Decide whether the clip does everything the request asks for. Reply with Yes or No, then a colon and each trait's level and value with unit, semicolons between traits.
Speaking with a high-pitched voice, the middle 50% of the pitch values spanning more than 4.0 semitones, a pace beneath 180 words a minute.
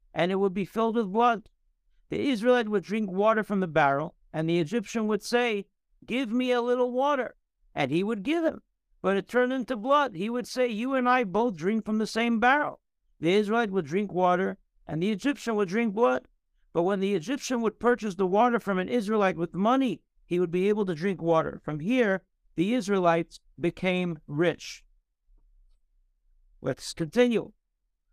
No: high, 210 Hz; average, 5.1 semitones; average, 185 wpm